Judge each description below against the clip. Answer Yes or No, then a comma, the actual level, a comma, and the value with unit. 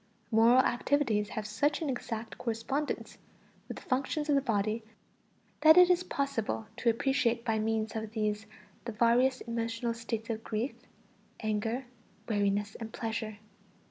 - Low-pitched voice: No, high, 230 Hz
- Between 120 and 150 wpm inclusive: Yes, average, 140 wpm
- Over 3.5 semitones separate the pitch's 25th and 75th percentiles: No, average, 2.9 semitones